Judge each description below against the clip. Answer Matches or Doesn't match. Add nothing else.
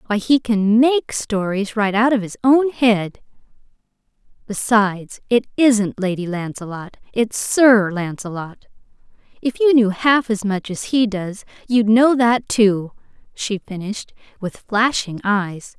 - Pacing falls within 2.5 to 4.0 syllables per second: Matches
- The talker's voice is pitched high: Matches